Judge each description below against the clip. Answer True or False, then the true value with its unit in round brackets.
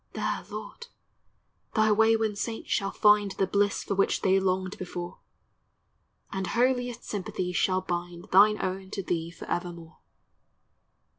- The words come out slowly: True (130 wpm)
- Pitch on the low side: False (195 Hz)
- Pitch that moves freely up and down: False (2.9 semitones)